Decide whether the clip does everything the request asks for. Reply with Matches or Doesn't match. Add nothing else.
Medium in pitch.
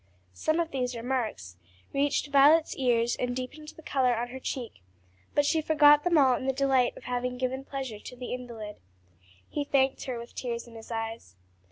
Doesn't match